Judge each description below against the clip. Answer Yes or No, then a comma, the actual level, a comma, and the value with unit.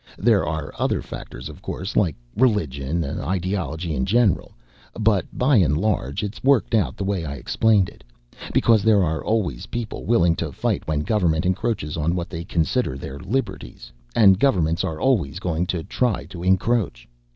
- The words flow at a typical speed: Yes, average, 170 wpm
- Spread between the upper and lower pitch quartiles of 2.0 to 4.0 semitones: No, wide, 5.4 semitones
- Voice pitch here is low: Yes, very low, 90 Hz